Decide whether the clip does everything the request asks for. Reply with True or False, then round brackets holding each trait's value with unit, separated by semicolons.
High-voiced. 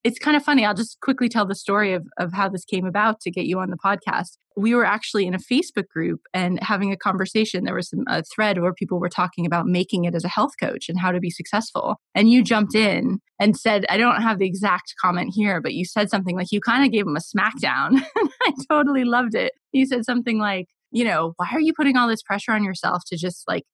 True (210 Hz)